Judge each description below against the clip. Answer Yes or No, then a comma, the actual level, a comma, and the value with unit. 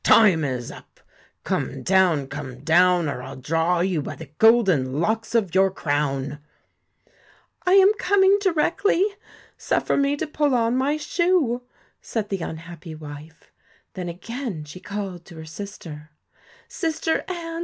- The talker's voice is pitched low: No, medium, 185 Hz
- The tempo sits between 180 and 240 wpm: No, average, 150 wpm